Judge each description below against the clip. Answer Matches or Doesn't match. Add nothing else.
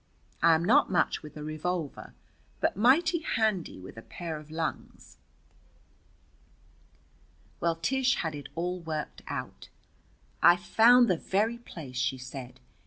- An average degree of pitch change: Doesn't match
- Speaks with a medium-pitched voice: Matches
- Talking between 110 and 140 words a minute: Matches